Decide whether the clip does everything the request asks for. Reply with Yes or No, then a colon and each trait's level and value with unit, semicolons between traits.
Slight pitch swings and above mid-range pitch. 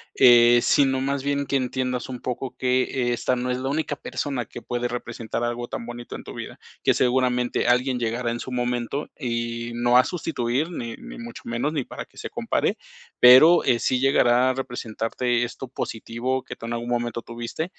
No: narrow, 1.8 semitones; low, 125 Hz